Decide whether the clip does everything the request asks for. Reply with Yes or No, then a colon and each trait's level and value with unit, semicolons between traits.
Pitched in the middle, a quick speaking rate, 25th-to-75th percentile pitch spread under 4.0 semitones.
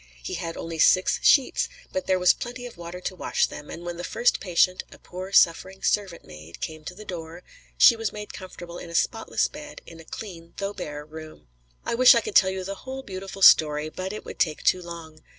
Yes: medium, 180 Hz; fast, 225 wpm; average, 3.5 semitones